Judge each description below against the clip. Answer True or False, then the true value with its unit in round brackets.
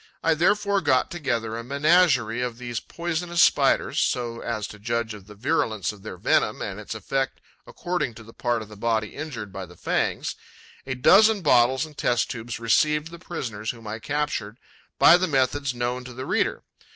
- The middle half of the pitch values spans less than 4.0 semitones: False (5.4 semitones)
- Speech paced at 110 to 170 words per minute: False (190 wpm)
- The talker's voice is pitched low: True (120 Hz)